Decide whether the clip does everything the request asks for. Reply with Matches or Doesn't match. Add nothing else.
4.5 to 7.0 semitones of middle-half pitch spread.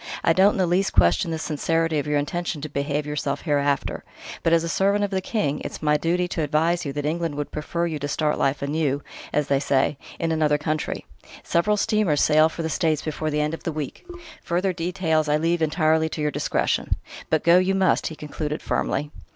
Doesn't match